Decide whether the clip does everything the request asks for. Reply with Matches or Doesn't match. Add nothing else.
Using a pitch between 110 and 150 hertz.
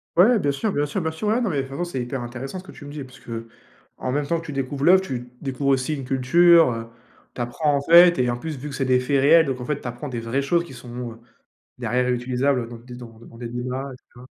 Matches